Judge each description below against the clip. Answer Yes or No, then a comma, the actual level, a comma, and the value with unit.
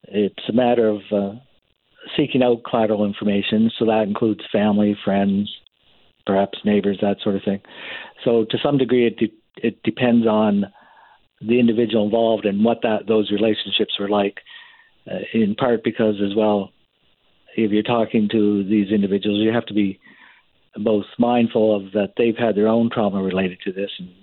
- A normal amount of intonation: No, narrow, 2.2 semitones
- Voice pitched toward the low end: Yes, low, 110 Hz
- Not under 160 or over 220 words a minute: Yes, average, 170 wpm